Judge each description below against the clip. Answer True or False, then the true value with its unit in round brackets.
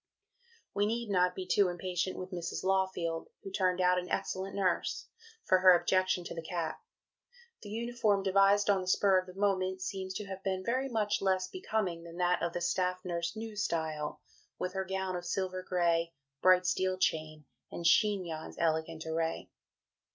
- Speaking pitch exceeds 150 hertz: True (185 Hz)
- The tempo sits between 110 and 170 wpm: False (180 wpm)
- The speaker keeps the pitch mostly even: True (2.1 semitones)